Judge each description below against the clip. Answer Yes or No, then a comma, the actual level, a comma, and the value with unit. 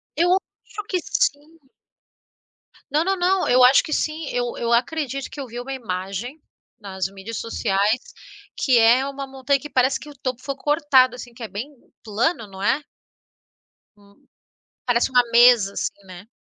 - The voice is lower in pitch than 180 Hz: No, very high, 255 Hz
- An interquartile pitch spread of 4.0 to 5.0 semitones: Yes, average, 4.5 semitones